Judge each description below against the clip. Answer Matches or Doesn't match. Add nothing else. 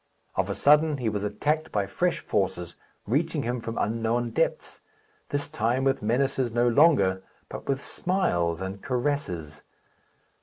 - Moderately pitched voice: Doesn't match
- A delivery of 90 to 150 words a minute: Matches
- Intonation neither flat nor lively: Doesn't match